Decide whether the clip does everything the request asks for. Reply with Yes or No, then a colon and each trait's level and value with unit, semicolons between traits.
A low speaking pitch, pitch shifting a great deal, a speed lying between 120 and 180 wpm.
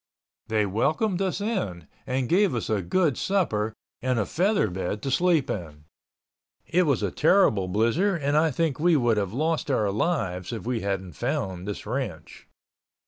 Yes: low, 125 Hz; wide, 8.5 semitones; average, 170 wpm